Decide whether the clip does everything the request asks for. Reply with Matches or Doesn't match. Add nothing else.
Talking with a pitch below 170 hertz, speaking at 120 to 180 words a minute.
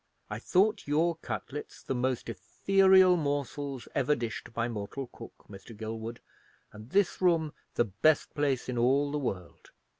Matches